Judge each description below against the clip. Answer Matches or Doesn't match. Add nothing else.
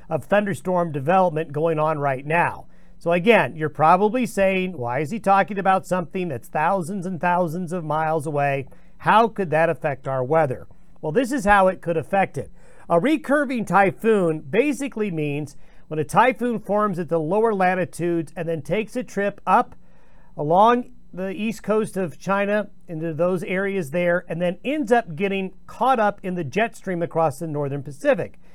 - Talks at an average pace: Matches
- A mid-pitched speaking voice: Matches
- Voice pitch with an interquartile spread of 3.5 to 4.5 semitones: Matches